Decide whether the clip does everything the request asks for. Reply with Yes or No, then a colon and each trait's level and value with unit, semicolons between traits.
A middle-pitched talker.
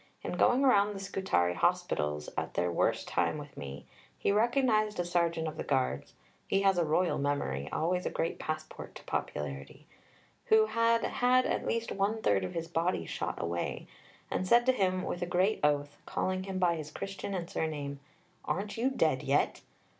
Yes: medium, 175 Hz